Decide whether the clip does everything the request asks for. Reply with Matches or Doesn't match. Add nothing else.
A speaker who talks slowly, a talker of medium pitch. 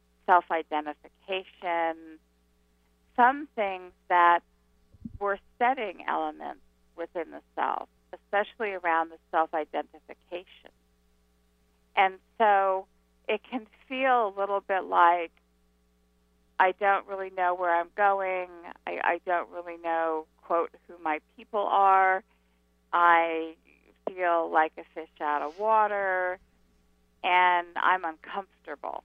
Matches